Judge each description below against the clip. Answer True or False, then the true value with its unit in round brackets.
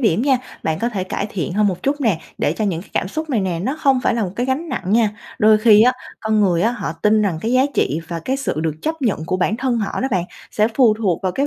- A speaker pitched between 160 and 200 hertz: False (215 Hz)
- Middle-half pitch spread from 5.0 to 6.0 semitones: True (5.4 semitones)